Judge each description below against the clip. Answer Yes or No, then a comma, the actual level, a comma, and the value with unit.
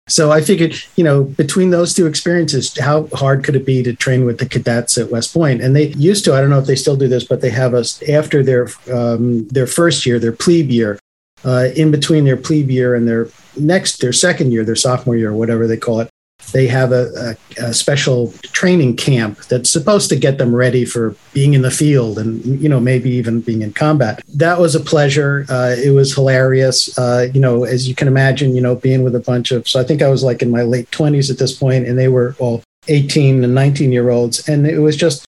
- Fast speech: Yes, fast, 235 wpm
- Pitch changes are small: No, average, 3.4 semitones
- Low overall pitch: Yes, low, 130 Hz